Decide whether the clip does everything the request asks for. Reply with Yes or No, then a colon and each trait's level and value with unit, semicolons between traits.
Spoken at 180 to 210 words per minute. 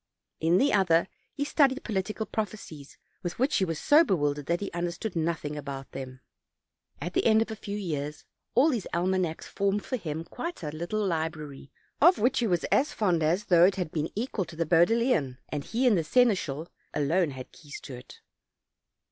Yes: average, 200 wpm